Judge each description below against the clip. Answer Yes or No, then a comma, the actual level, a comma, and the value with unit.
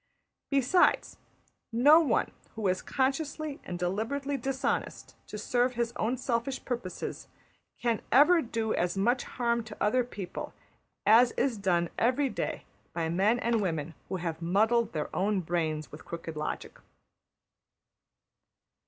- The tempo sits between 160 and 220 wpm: No, slow, 135 wpm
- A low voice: No, high, 230 Hz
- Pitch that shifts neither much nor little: No, wide, 6.1 semitones